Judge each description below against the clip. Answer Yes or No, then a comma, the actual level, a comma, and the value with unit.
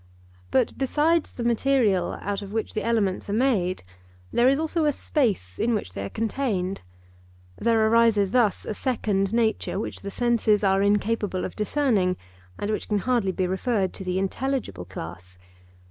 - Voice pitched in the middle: No, high, 215 Hz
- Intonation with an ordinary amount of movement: Yes, average, 3.9 semitones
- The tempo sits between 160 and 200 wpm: Yes, average, 165 wpm